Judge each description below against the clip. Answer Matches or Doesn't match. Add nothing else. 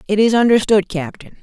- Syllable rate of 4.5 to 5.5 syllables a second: Doesn't match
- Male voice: Doesn't match